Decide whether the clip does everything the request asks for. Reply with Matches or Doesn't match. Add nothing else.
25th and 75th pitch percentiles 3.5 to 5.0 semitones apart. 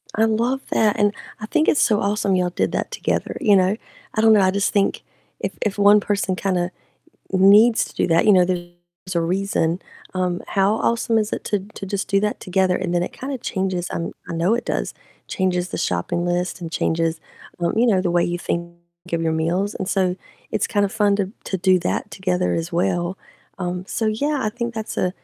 Doesn't match